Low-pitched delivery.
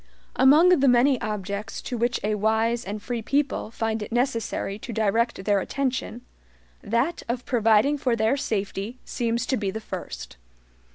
No: high, 230 Hz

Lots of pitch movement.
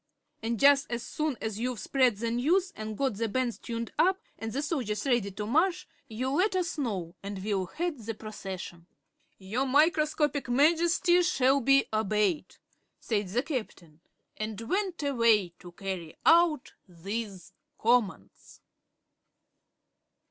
Yes: wide, 6.0 semitones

